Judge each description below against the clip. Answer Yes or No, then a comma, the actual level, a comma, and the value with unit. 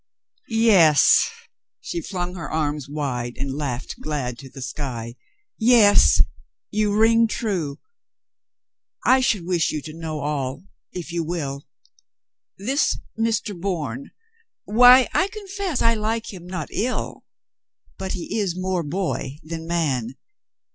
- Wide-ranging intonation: Yes, wide, 7.2 semitones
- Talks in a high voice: No, medium, 175 Hz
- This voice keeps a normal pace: No, slow, 125 wpm